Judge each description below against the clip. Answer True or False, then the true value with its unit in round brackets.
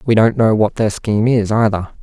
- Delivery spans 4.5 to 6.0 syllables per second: True (5.4 syllables/s)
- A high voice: False (110 Hz)